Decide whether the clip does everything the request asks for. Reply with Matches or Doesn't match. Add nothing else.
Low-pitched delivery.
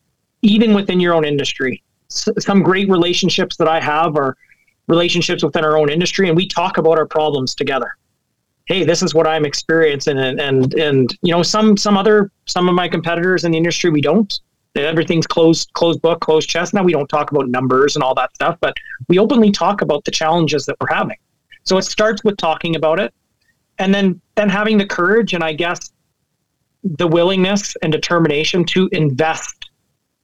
Doesn't match